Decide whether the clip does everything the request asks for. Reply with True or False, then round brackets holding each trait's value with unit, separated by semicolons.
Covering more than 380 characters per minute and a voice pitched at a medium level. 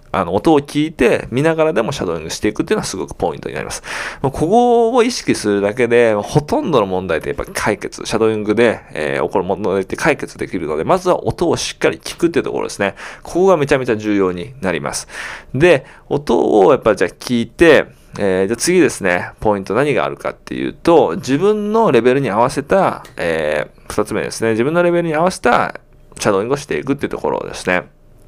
True (450 characters per minute; 145 Hz)